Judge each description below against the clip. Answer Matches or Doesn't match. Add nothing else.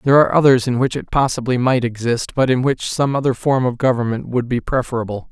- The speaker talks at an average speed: Doesn't match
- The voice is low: Matches